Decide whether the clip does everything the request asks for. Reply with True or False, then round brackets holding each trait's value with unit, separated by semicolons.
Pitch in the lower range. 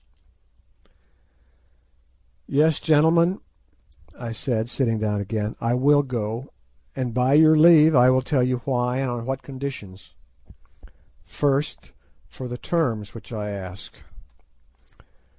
True (125 Hz)